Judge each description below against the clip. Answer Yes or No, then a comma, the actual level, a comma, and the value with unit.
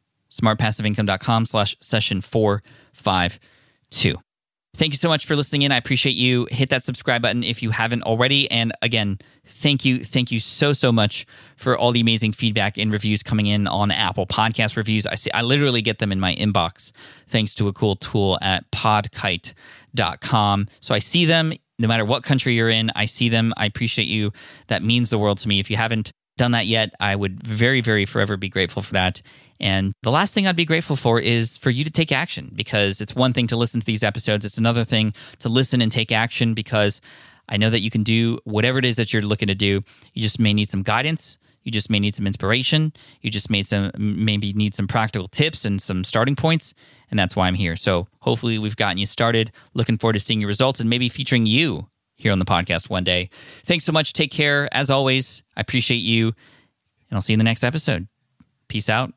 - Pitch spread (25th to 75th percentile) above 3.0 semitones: Yes, average, 3.4 semitones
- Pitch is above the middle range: No, low, 115 Hz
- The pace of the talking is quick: Yes, fast, 220 wpm